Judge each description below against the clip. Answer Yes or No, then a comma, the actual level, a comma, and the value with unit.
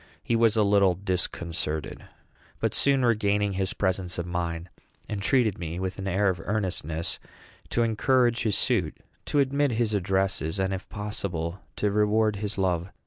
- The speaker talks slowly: No, average, 155 wpm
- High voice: No, low, 100 Hz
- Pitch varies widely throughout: No, average, 3.3 semitones